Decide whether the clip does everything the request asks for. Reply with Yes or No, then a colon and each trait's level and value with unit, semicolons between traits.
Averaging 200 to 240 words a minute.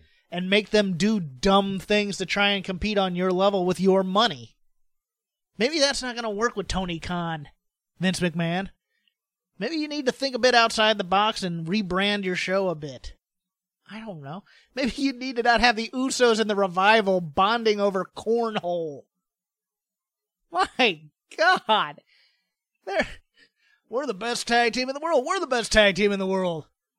No: average, 175 wpm